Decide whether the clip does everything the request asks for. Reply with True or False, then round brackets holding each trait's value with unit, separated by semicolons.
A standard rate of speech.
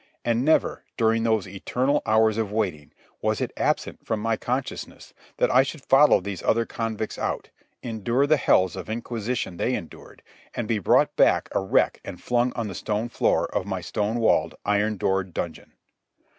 True (175 wpm)